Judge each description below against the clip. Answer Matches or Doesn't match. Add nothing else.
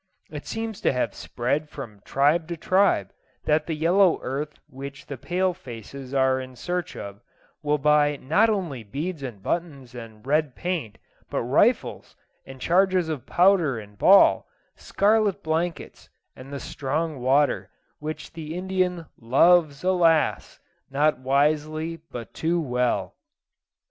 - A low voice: Doesn't match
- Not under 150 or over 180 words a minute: Doesn't match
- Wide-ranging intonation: Doesn't match